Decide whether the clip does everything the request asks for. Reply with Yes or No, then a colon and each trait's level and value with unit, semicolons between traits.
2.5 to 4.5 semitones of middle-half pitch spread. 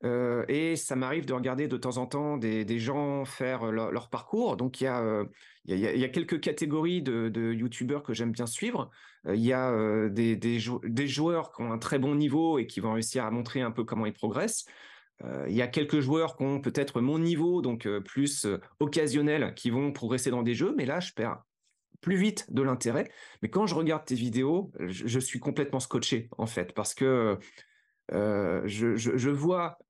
Yes: average, 4.2 semitones